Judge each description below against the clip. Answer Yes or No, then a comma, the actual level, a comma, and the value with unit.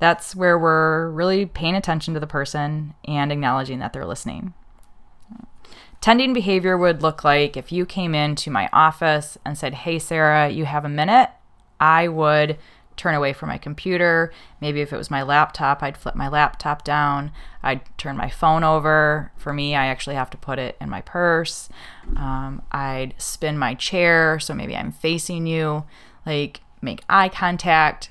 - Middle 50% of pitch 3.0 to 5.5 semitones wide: No, narrow, 2.6 semitones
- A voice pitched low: No, medium, 155 Hz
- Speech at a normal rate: Yes, average, 175 wpm